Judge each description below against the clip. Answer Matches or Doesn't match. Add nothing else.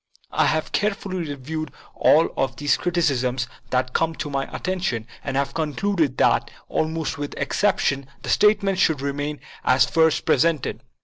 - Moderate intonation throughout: Matches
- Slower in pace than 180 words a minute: Matches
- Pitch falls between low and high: Matches